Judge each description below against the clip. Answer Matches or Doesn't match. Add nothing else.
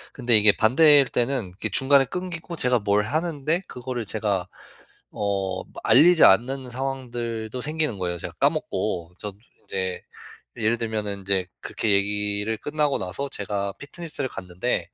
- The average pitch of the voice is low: Matches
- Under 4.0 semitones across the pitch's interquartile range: Doesn't match